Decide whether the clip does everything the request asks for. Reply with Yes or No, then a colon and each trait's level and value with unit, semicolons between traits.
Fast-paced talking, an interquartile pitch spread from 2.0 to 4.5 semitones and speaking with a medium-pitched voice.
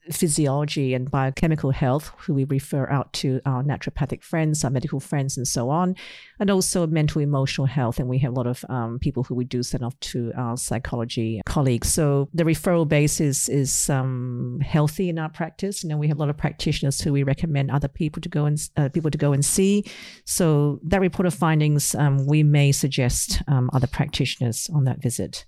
Yes: fast, 210 wpm; average, 3.2 semitones; medium, 145 Hz